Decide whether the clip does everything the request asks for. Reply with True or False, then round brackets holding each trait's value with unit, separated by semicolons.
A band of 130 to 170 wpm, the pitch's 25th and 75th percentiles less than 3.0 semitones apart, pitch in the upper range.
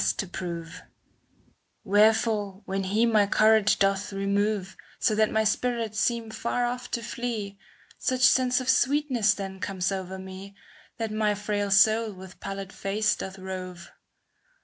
True (150 wpm; 2.5 semitones; 205 Hz)